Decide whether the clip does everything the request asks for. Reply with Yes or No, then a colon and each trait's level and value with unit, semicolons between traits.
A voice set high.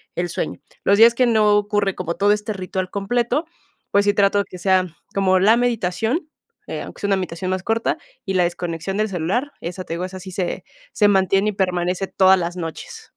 Yes: high, 195 Hz